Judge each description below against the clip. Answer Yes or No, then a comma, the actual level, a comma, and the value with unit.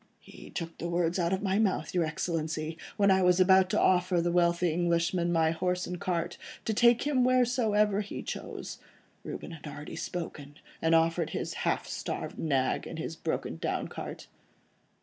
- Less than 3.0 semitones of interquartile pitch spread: Yes, narrow, 2.6 semitones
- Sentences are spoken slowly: No, average, 175 wpm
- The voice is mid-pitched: Yes, medium, 175 Hz